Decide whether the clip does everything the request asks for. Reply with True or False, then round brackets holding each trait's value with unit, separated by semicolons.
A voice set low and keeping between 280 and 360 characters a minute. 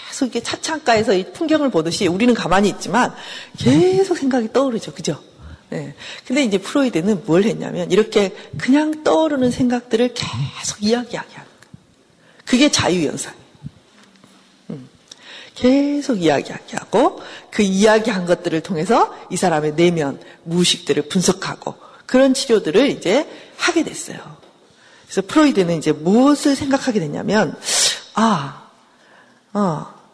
False (230 Hz; 305 characters per minute)